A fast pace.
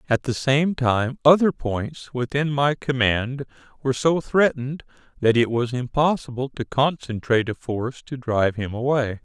No: average, 155 wpm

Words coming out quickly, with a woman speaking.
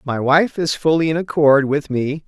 No: fast, 210 wpm; male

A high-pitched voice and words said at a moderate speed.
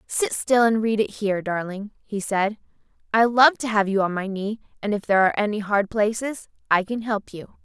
No: high, 210 Hz; fast, 220 wpm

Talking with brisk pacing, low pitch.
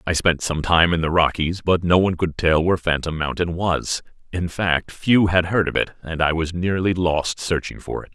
Yes: fast, 230 wpm; very low, 85 Hz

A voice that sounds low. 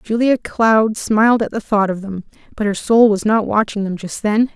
No: high, 215 Hz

